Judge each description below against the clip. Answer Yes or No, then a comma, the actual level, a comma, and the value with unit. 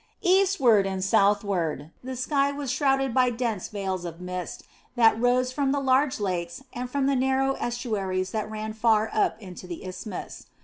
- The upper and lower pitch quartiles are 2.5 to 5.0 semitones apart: No, wide, 5.5 semitones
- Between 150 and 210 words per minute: Yes, average, 170 wpm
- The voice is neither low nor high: No, high, 225 Hz